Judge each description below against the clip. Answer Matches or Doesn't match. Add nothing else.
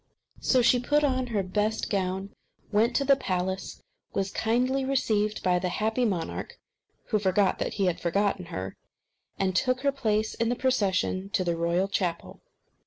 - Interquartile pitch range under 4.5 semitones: Doesn't match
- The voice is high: Matches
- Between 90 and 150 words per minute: Doesn't match